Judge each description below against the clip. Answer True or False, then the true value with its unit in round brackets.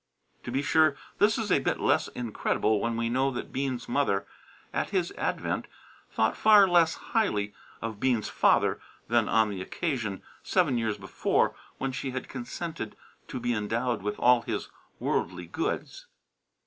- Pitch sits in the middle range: False (125 Hz)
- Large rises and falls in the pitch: False (4.7 semitones)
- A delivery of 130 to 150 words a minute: False (160 wpm)